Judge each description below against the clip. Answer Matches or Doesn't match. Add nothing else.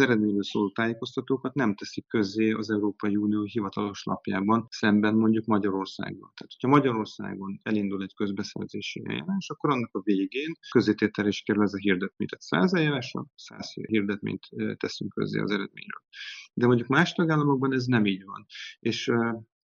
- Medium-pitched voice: Doesn't match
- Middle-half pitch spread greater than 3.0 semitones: Matches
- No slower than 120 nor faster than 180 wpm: Matches